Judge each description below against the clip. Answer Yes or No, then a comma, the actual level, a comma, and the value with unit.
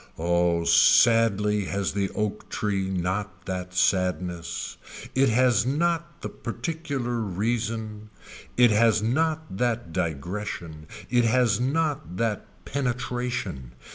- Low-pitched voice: Yes, low, 105 Hz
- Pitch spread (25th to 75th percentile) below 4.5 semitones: No, average, 5.0 semitones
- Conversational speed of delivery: No, slow, 110 wpm